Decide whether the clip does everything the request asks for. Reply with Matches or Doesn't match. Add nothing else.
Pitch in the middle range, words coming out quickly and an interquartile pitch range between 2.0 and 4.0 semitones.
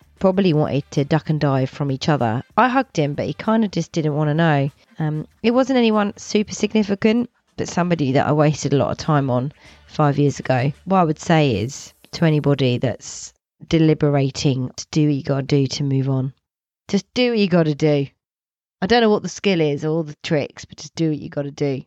Doesn't match